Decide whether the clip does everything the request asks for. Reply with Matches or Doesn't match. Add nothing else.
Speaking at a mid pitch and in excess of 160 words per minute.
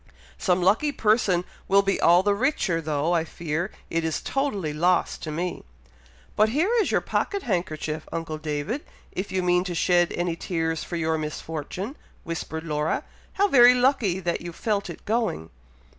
Matches